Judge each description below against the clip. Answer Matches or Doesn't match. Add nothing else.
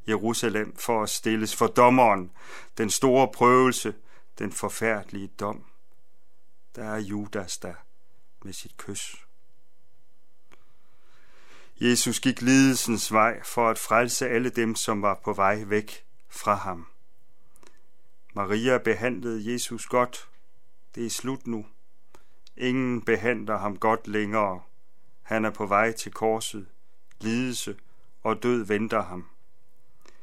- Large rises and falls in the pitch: Doesn't match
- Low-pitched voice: Matches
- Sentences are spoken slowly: Matches